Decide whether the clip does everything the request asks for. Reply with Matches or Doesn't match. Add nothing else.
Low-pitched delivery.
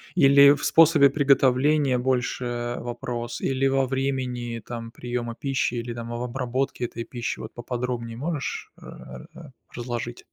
Matches